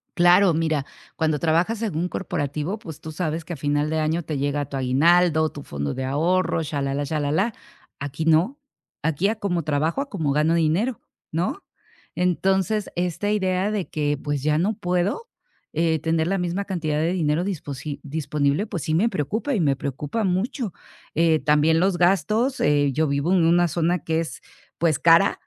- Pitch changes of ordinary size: Yes, average, 3.7 semitones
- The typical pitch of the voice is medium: Yes, medium, 165 Hz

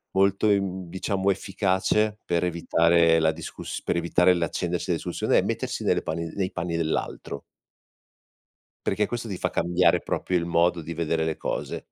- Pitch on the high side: No, very low, 90 Hz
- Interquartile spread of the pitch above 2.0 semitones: Yes, narrow, 2.5 semitones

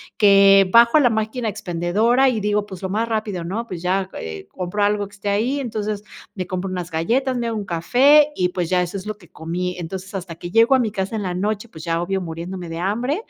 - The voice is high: Yes, high, 200 Hz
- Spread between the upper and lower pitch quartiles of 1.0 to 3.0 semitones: No, average, 3.9 semitones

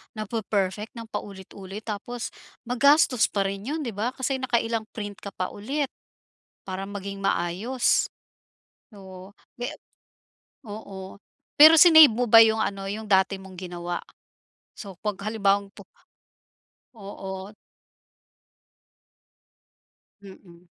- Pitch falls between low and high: No, high, 205 Hz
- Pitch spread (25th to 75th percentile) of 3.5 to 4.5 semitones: No, average, 3.1 semitones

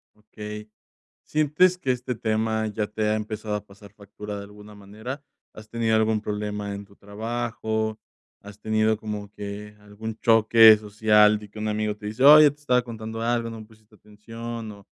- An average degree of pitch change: No, narrow, 1.4 semitones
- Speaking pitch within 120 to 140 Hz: No, low, 110 Hz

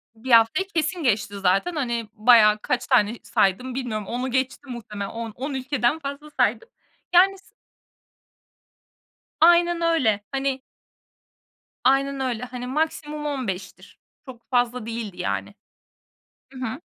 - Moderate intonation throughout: Yes, average, 4.0 semitones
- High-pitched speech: Yes, very high, 255 Hz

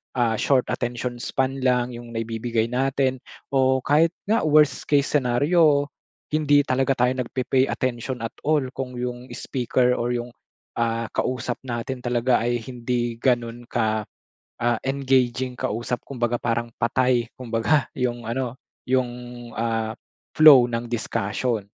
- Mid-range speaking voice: No, low, 125 Hz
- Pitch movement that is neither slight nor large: No, narrow, 2.0 semitones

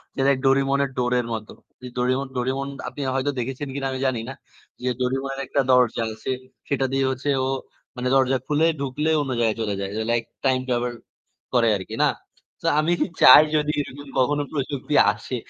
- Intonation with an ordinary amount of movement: No, narrow, 2.0 semitones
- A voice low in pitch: Yes, low, 130 Hz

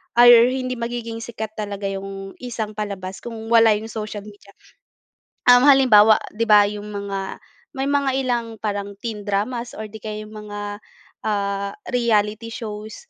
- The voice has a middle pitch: No, high, 215 Hz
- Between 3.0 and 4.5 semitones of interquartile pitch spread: No, narrow, 2.4 semitones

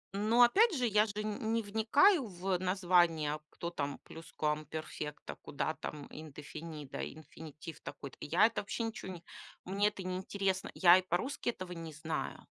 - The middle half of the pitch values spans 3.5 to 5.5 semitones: Yes, average, 5.1 semitones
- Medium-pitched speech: Yes, medium, 180 Hz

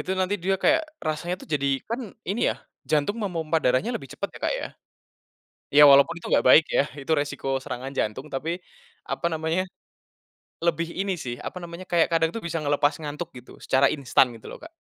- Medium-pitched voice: Yes, medium, 160 Hz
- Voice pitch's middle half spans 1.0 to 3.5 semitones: No, average, 4.5 semitones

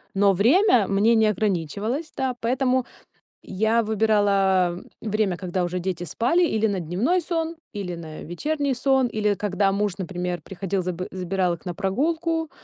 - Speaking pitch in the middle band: No, high, 205 Hz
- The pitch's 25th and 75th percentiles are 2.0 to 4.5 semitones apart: No, wide, 5.4 semitones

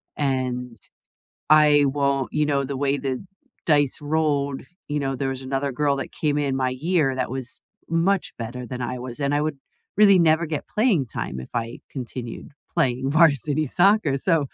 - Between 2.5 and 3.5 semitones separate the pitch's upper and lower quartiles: Yes, average, 2.8 semitones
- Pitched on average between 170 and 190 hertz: No, medium, 140 Hz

